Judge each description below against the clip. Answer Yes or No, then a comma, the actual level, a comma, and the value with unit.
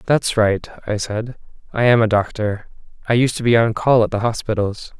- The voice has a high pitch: No, low, 110 Hz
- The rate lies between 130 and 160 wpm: No, fast, 205 wpm